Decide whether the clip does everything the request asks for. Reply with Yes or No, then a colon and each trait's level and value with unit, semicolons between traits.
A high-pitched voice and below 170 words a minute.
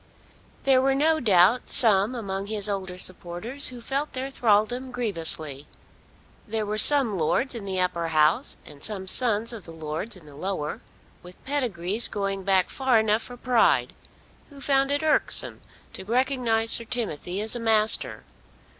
Yes: high, 215 Hz; average, 160 wpm